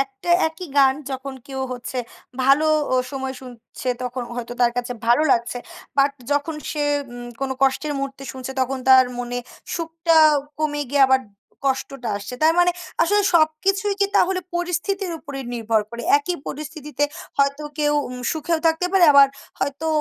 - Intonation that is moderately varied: Yes, average, 3.8 semitones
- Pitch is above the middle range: Yes, very high, 275 Hz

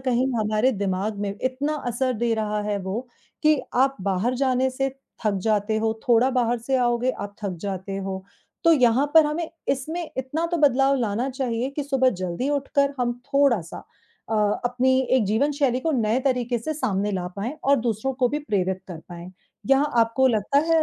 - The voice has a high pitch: Yes, high, 245 Hz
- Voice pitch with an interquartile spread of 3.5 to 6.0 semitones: Yes, average, 4.4 semitones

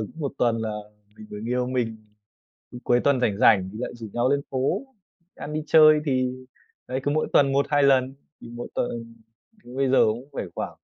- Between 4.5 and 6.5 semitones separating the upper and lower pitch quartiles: No, average, 3.1 semitones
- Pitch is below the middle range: Yes, low, 125 Hz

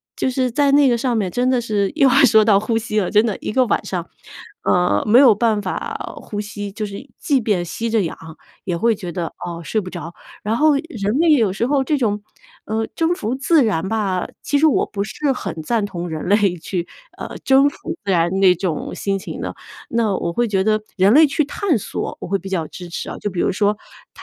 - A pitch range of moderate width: Yes, average, 4.7 semitones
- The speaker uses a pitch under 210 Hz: No, high, 215 Hz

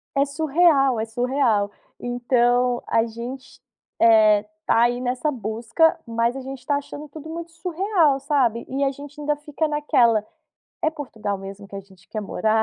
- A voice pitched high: Yes, very high, 250 Hz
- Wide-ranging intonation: No, average, 4.4 semitones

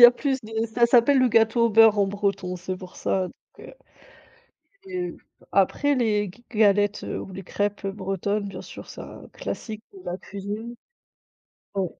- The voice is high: Yes, high, 210 Hz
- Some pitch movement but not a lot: Yes, average, 3.2 semitones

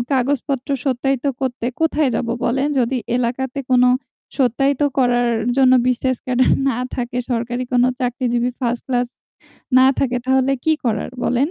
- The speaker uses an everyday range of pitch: No, narrow, 1.6 semitones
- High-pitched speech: Yes, very high, 255 Hz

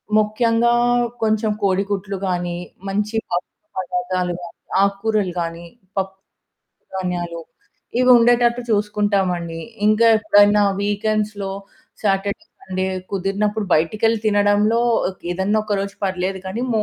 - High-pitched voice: Yes, high, 205 Hz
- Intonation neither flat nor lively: No, narrow, 2.3 semitones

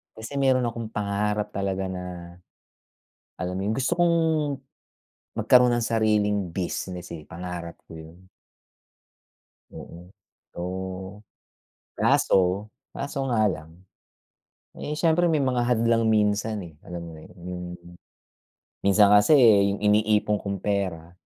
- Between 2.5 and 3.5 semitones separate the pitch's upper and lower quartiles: No, average, 4.0 semitones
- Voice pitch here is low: Yes, low, 105 Hz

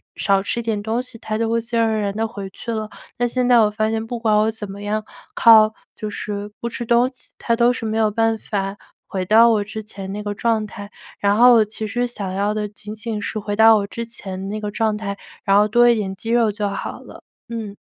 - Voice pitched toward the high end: Yes, high, 215 Hz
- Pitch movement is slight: Yes, narrow, 1.9 semitones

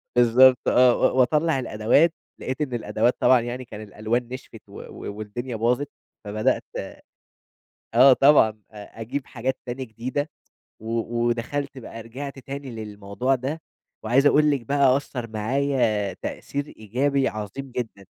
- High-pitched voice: No, low, 125 Hz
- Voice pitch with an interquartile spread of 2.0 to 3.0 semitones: No, average, 3.5 semitones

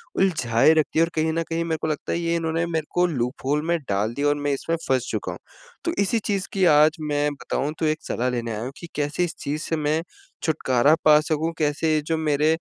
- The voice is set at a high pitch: No, medium, 155 Hz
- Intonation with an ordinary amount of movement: No, narrow, 2.3 semitones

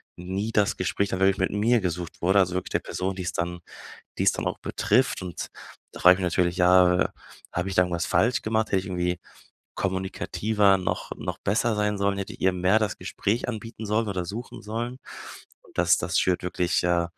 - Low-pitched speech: Yes, very low, 95 Hz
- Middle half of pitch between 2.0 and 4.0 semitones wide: Yes, average, 2.7 semitones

